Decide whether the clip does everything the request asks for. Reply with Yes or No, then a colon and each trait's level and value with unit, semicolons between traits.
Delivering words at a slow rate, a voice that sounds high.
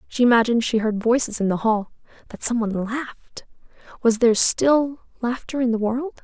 No: average, 165 wpm; high, 235 Hz